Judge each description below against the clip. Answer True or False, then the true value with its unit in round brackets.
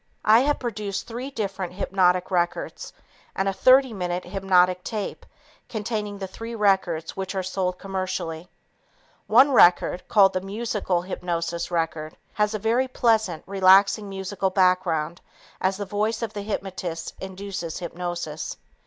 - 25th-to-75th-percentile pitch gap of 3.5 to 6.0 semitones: False (2.8 semitones)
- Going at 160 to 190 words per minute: False (135 wpm)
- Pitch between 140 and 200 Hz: True (190 Hz)